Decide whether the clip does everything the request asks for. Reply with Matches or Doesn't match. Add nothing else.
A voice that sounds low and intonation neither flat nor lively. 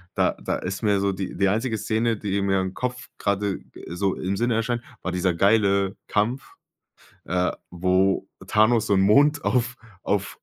Matches